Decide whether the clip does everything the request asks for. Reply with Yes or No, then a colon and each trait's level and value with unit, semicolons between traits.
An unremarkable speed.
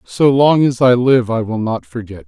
No: fast, 235 wpm